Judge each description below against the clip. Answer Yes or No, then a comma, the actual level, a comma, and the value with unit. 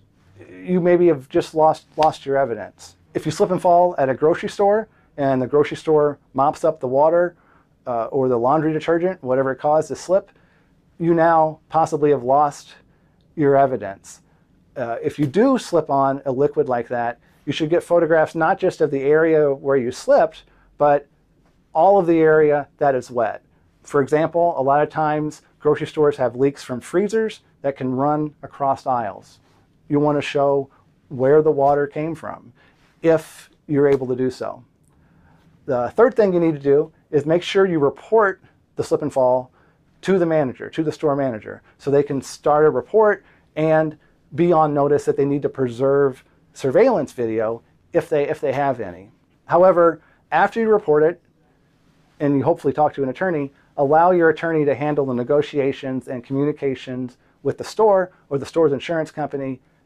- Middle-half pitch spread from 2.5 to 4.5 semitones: Yes, average, 2.8 semitones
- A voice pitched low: No, medium, 150 Hz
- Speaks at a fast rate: No, average, 180 wpm